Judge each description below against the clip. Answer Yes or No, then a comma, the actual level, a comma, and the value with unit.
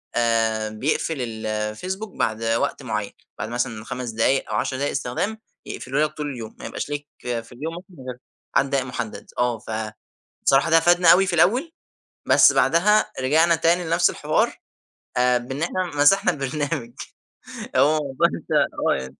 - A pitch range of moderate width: No, wide, 5.9 semitones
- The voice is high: No, low, 135 Hz